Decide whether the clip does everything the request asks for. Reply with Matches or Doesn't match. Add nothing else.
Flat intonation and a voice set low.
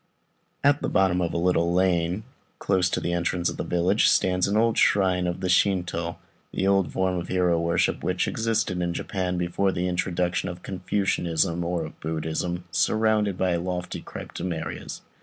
Matches